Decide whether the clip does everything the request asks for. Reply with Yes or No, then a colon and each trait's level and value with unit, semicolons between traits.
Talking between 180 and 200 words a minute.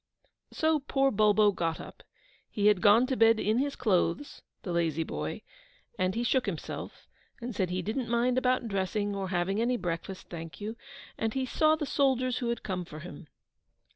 Yes: average, 185 wpm